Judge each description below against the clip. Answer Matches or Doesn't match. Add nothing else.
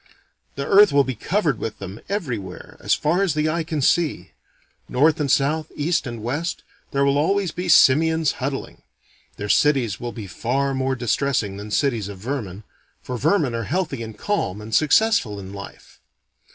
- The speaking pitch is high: Doesn't match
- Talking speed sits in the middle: Matches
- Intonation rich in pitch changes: Matches